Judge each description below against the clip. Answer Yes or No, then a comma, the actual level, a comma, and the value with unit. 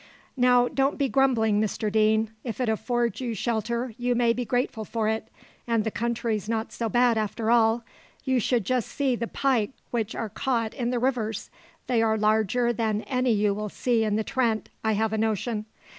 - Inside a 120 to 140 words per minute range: No, average, 195 wpm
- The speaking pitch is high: Yes, high, 230 Hz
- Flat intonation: Yes, narrow, 2.1 semitones